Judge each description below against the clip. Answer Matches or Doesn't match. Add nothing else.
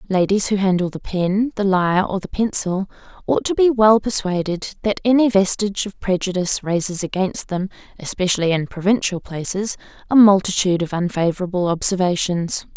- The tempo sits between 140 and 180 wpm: Matches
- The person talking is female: Matches